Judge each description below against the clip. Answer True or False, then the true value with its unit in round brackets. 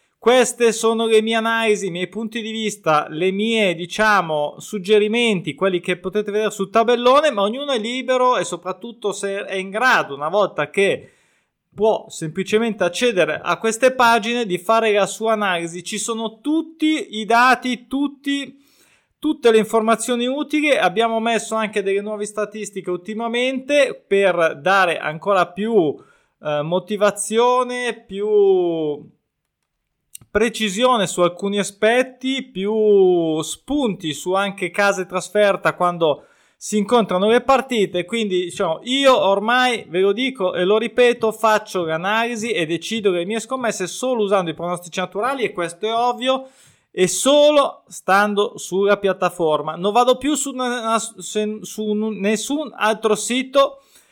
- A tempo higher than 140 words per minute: False (135 wpm)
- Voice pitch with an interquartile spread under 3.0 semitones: False (4.1 semitones)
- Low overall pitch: False (215 Hz)